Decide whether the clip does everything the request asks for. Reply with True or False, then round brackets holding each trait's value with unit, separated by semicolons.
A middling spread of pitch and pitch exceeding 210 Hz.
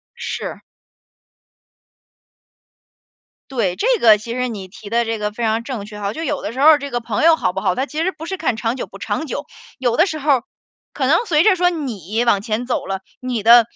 False (5.7 semitones; 240 Hz)